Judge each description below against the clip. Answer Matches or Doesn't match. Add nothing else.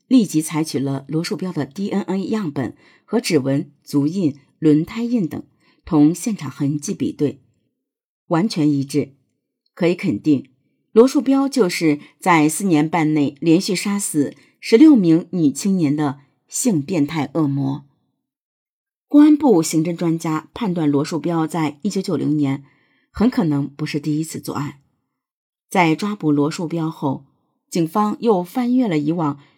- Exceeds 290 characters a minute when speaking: Doesn't match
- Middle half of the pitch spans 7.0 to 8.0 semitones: Doesn't match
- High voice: Doesn't match